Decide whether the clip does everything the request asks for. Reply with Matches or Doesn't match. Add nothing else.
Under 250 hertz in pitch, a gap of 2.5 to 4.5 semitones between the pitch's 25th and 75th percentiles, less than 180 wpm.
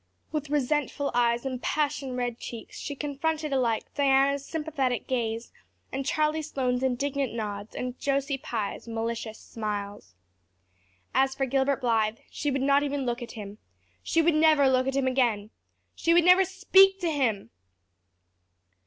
Doesn't match